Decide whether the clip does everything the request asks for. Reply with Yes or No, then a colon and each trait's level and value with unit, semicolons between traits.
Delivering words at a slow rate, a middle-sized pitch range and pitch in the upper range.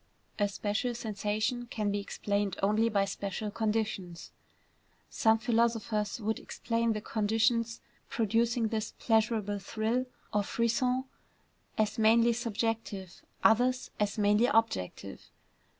No: slow, 110 wpm; narrow, 1.9 semitones; high, 220 Hz